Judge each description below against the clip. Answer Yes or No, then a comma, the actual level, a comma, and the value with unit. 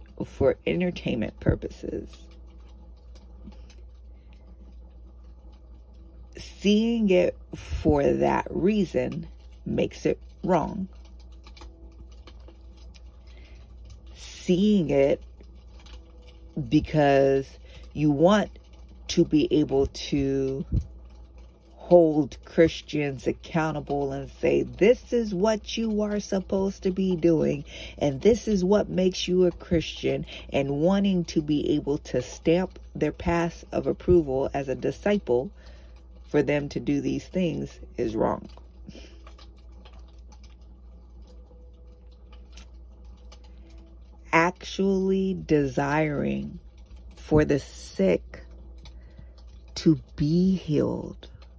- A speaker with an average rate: No, slow, 85 wpm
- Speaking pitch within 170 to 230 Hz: No, very low, 70 Hz